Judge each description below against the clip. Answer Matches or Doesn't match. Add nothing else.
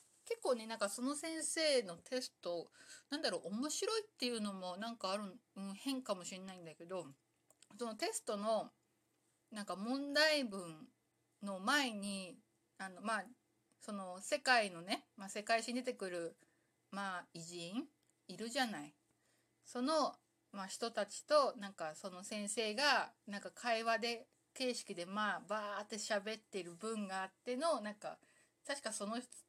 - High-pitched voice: Matches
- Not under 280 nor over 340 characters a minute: Matches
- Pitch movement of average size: Matches